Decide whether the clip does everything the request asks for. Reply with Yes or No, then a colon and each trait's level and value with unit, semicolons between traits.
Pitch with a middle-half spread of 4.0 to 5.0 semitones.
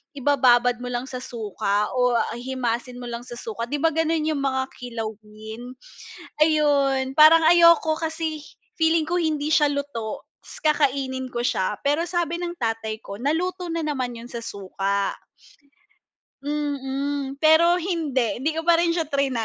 Yes: average, 4.7 semitones